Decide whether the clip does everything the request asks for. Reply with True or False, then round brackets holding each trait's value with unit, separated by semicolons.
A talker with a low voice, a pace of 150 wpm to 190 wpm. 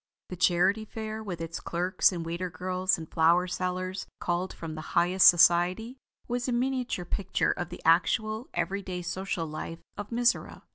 False (185 Hz; 170 wpm)